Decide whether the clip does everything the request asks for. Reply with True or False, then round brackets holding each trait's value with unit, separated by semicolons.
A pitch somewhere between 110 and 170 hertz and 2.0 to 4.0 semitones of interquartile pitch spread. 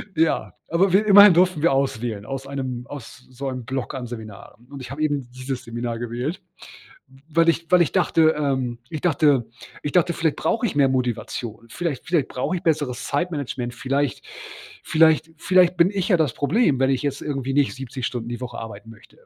False (140 Hz; 4.8 semitones)